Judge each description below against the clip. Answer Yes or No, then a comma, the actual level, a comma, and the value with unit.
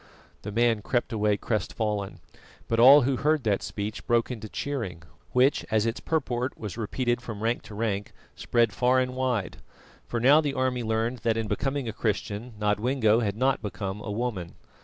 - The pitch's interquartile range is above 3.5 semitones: No, average, 3.2 semitones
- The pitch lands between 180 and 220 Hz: No, low, 115 Hz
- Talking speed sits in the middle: Yes, average, 180 wpm